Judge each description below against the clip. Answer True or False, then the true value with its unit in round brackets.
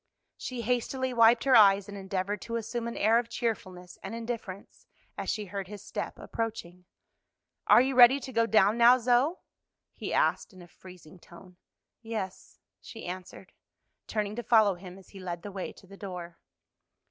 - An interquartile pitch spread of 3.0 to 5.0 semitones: True (3.8 semitones)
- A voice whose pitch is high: True (210 Hz)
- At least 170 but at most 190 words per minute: True (175 wpm)